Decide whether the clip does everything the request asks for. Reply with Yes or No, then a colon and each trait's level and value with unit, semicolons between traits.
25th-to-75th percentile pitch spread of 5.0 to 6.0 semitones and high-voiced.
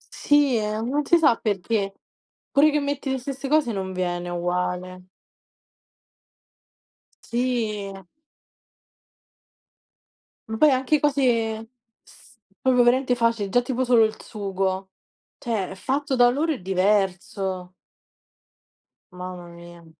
Yes: wide, 5.6 semitones; high, 225 Hz